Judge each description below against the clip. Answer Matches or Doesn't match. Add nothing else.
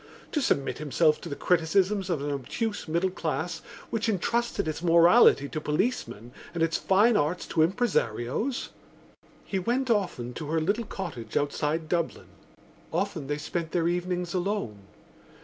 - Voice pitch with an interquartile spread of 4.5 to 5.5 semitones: Matches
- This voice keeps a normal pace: Matches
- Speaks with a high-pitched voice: Doesn't match